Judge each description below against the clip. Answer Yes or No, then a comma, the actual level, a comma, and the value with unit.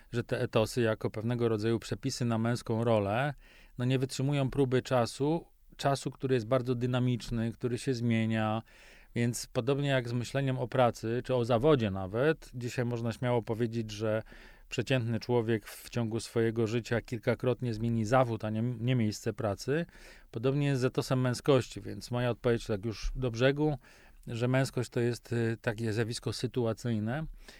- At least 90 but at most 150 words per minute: No, fast, 160 wpm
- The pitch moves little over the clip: Yes, narrow, 2.2 semitones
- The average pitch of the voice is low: Yes, low, 120 Hz